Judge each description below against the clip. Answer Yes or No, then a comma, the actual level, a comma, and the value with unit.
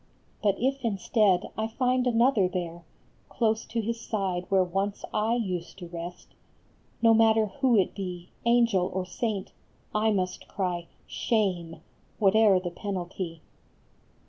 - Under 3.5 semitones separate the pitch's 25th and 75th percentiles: No, average, 3.8 semitones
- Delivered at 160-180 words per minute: No, average, 145 wpm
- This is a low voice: No, high, 200 Hz